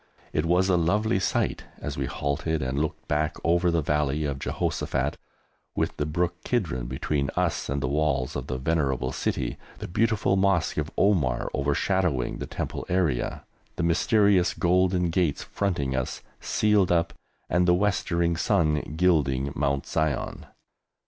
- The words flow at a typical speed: Yes, average, 150 wpm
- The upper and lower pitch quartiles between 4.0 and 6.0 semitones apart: Yes, average, 4.3 semitones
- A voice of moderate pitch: No, very low, 80 Hz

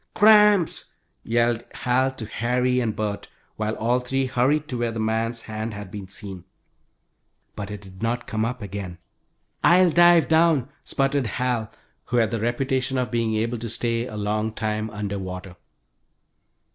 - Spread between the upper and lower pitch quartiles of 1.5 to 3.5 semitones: Yes, average, 3.0 semitones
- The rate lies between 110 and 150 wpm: No, average, 160 wpm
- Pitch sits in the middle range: No, low, 115 Hz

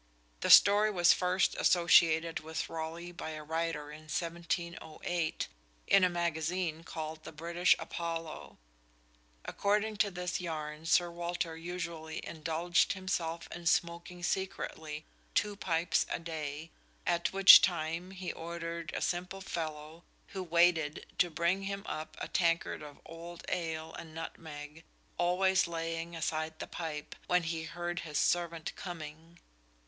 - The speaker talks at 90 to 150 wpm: Yes, slow, 135 wpm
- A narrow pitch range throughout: Yes, narrow, 1.7 semitones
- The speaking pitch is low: No, medium, 170 Hz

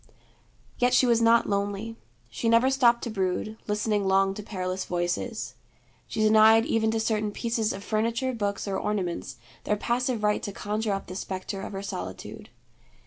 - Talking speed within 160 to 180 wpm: Yes, average, 170 wpm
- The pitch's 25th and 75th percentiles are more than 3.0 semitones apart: No, average, 2.7 semitones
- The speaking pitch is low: No, high, 215 Hz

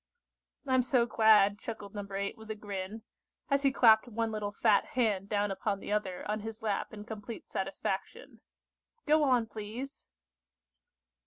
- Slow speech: No, average, 155 wpm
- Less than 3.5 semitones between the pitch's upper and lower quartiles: Yes, narrow, 2.5 semitones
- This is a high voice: Yes, high, 215 Hz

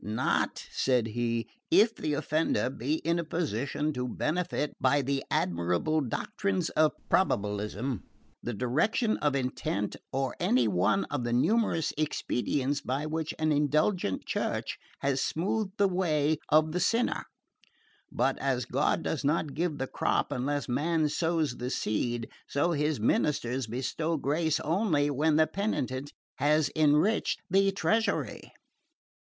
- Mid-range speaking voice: Yes, medium, 150 Hz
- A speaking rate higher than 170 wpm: No, slow, 135 wpm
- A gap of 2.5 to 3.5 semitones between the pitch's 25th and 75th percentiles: No, average, 4.3 semitones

